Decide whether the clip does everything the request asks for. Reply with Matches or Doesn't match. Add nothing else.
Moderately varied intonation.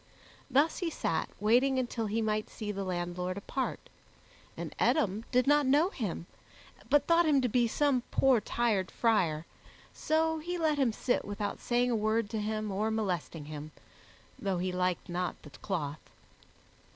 Doesn't match